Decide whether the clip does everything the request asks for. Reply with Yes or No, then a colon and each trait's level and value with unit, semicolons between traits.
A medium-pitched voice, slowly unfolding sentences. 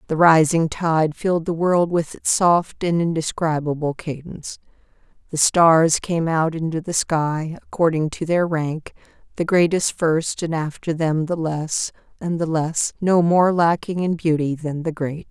No: medium, 160 Hz; average, 160 wpm